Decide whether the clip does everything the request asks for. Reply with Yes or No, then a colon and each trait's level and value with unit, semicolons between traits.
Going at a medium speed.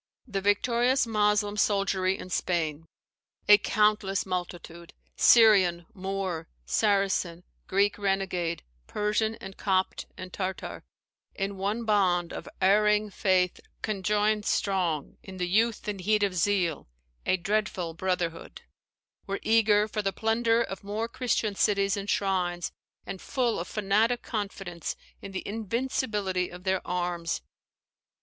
No: slow, 125 wpm